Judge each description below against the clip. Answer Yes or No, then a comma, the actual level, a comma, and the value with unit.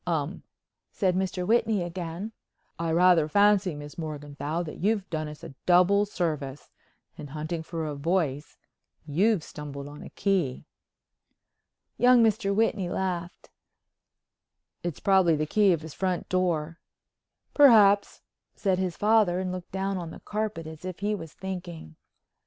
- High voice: No, medium, 175 Hz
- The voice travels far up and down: No, average, 4.0 semitones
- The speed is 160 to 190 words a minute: No, average, 140 wpm